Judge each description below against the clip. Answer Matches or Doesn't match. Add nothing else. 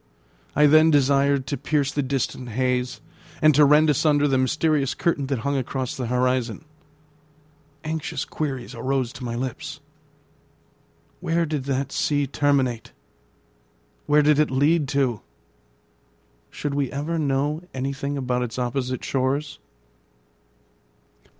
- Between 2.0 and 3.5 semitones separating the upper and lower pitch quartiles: Matches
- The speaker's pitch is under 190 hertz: Matches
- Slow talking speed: Matches